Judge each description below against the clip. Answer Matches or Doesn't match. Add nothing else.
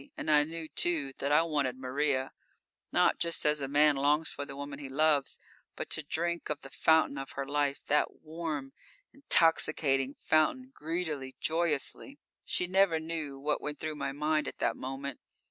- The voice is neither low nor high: Matches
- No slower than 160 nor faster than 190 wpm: Matches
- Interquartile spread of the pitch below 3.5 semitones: Matches